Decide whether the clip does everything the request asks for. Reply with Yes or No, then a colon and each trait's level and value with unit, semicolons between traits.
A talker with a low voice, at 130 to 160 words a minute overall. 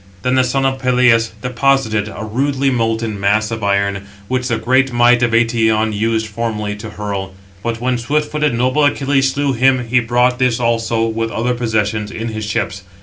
No: low, 115 Hz; average, 185 wpm